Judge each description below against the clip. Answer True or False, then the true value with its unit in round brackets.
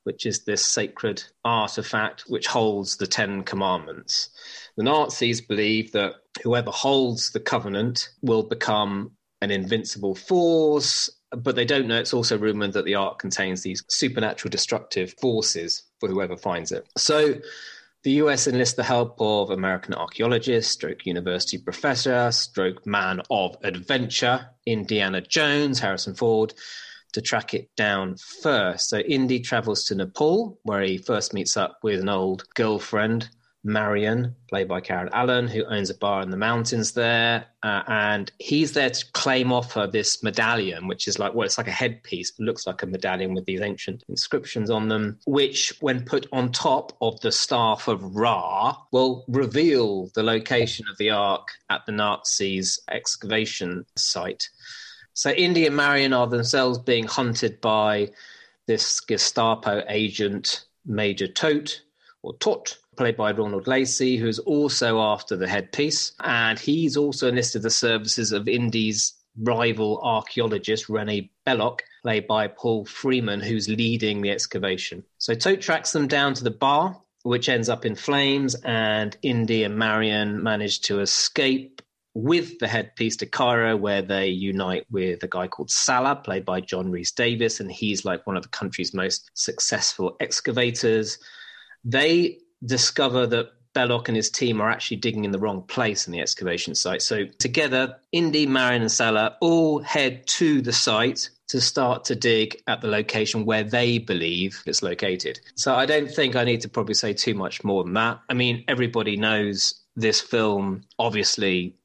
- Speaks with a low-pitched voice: True (115 Hz)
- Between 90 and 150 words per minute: False (160 wpm)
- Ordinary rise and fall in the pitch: True (3.5 semitones)